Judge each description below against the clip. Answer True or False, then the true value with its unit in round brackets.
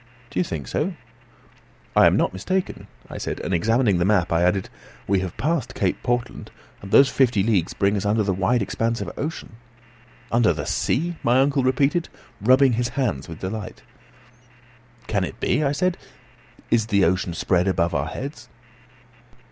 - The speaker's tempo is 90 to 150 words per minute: False (170 wpm)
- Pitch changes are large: True (5.9 semitones)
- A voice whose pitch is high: False (110 Hz)